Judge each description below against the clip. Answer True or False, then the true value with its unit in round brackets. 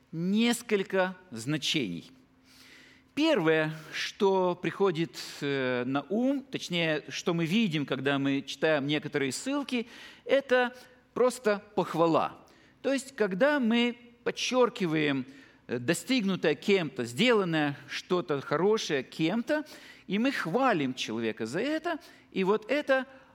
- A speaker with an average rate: False (100 wpm)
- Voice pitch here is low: False (190 Hz)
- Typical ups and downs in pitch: False (8.6 semitones)